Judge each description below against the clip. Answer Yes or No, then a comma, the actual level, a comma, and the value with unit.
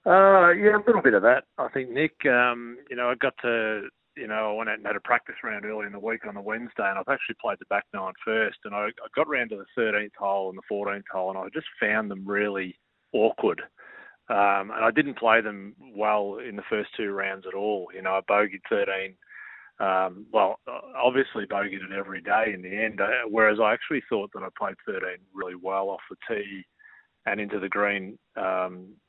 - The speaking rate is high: Yes, fast, 225 wpm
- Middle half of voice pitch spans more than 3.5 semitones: No, narrow, 2.6 semitones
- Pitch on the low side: Yes, low, 105 Hz